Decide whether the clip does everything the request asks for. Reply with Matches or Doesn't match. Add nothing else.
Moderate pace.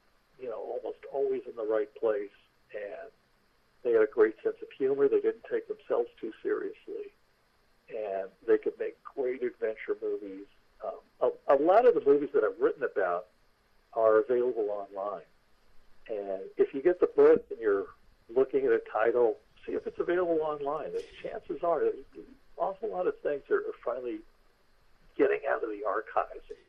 Matches